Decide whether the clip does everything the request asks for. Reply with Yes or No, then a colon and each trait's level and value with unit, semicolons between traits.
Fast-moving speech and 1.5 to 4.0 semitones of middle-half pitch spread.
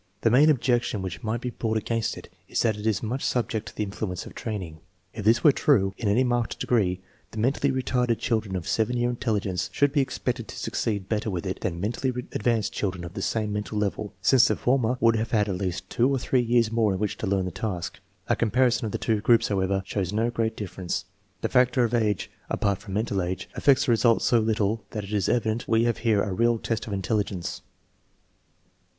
Yes: fast, 230 wpm; average, 3.1 semitones